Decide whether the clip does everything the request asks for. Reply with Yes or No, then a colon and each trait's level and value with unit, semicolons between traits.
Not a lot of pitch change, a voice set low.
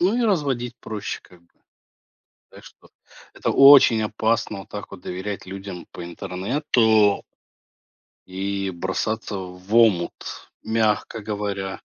No: average, 3.1 semitones; low, 105 Hz